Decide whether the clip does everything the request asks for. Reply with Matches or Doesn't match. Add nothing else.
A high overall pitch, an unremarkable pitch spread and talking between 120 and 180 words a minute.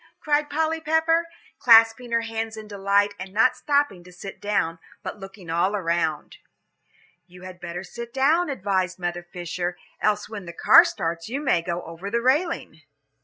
Doesn't match